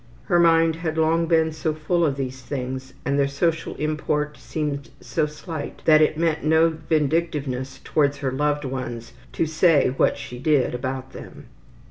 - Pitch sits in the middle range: Yes, medium, 150 Hz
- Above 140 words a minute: Yes, average, 165 wpm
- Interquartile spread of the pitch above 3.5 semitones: No, average, 3.1 semitones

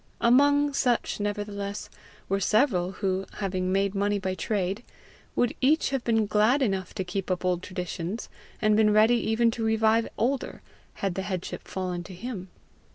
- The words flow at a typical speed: Yes, average, 160 wpm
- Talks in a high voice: Yes, high, 205 Hz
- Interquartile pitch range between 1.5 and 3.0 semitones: No, average, 3.4 semitones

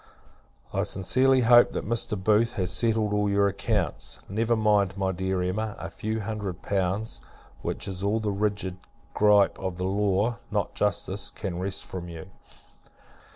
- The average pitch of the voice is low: Yes, low, 100 Hz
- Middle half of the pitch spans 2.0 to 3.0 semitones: Yes, narrow, 2.6 semitones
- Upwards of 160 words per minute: No, average, 155 wpm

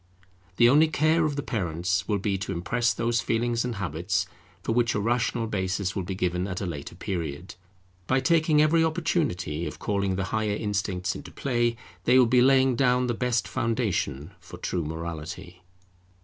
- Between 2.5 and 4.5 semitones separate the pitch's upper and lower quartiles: No, wide, 5.6 semitones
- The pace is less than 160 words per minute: No, average, 175 wpm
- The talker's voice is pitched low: Yes, low, 105 Hz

